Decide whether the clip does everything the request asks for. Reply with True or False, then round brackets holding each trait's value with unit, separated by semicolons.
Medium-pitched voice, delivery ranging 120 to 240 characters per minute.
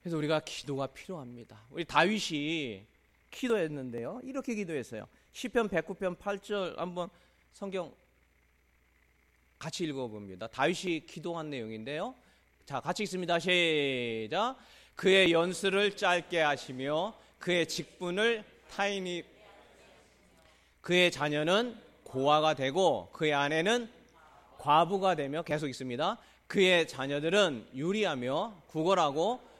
False (165 Hz; 255 characters per minute)